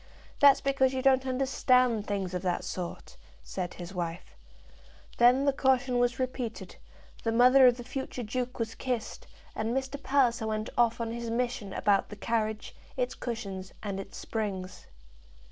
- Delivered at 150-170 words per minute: Yes, average, 160 wpm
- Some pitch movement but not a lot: Yes, average, 3.5 semitones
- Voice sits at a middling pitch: No, high, 235 Hz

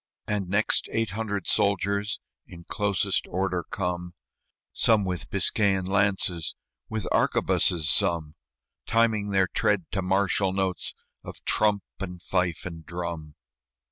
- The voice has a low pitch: Yes, very low, 95 Hz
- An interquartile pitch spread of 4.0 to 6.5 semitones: No, narrow, 2.5 semitones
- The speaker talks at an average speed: No, slow, 120 wpm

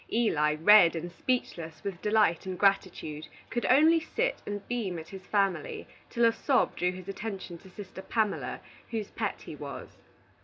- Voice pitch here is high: Yes, high, 195 Hz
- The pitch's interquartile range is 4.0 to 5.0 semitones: Yes, average, 4.5 semitones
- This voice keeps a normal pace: Yes, average, 165 wpm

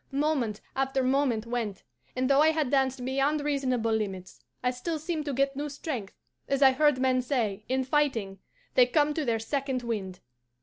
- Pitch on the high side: Yes, very high, 265 Hz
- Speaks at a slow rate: No, average, 185 wpm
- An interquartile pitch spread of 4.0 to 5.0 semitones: No, average, 3.5 semitones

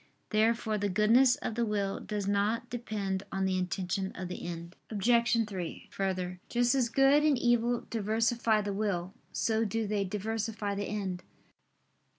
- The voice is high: Yes, high, 210 Hz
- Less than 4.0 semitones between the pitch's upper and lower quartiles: Yes, average, 3.0 semitones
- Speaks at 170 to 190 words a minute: No, average, 160 wpm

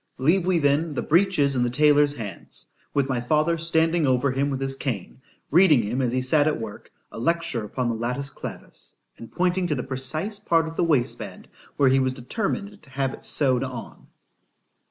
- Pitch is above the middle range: No, medium, 140 Hz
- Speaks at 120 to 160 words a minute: No, average, 200 wpm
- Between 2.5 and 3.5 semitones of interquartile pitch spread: No, average, 4.2 semitones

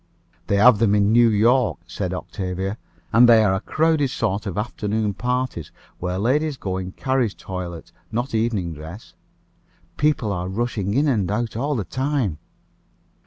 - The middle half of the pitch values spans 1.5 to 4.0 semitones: No, average, 4.7 semitones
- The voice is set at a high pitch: No, low, 110 Hz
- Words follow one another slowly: No, average, 160 wpm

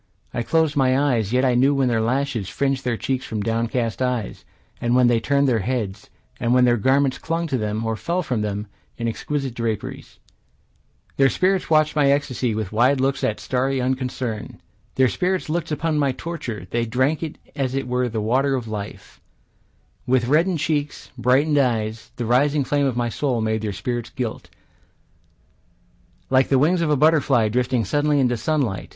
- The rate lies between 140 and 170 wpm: No, average, 180 wpm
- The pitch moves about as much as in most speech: Yes, average, 3.5 semitones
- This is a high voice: No, low, 130 Hz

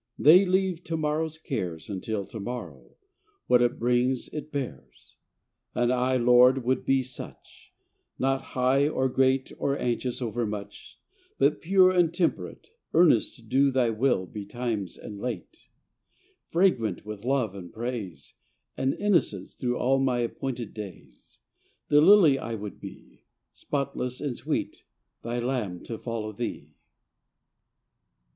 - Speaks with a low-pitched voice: Yes, low, 125 Hz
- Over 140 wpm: No, slow, 135 wpm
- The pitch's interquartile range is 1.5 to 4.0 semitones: Yes, average, 3.6 semitones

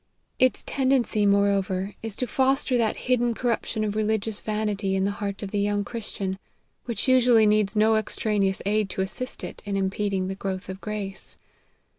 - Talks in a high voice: Yes, high, 210 Hz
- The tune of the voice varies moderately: No, narrow, 2.3 semitones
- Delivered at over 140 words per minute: Yes, average, 170 wpm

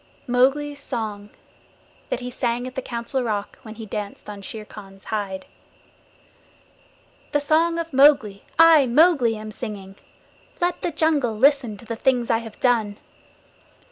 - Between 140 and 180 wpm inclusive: Yes, average, 145 wpm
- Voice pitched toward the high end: Yes, high, 240 Hz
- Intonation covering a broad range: No, average, 5.0 semitones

